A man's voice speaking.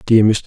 Yes: male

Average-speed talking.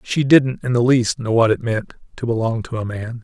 No: fast, 240 wpm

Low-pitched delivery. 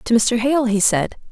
No: high, 230 Hz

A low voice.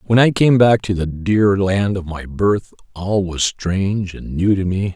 Yes: very low, 95 Hz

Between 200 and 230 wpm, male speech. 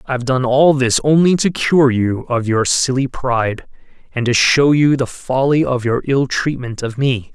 Yes: fast, 205 wpm; male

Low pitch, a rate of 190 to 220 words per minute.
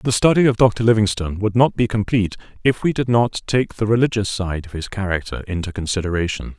Yes: low, 105 Hz; average, 200 wpm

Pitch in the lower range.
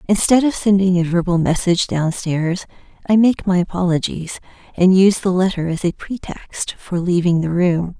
No: medium, 180 Hz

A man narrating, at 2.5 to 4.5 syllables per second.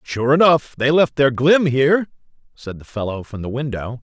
No: male; 5.0 syllables/s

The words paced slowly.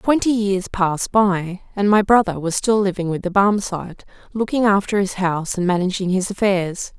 No: average, 180 wpm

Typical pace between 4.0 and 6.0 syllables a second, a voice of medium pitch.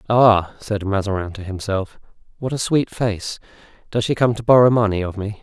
No: 5.1 syllables/s; low, 105 Hz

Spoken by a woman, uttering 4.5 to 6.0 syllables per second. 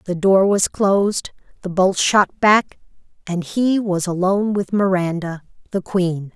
No: female; 4.1 syllables/s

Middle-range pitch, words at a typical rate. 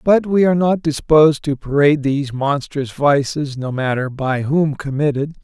Yes: medium, 145 Hz; average, 165 wpm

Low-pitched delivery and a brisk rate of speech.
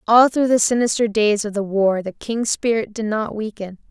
No: high, 220 Hz; fast, 215 wpm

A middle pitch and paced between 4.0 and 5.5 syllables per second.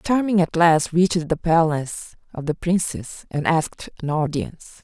Yes: medium, 165 Hz; 4.8 syllables/s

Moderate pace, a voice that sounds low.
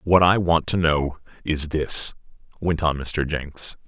Yes: average, 170 wpm; very low, 80 Hz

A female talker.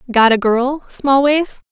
Yes: female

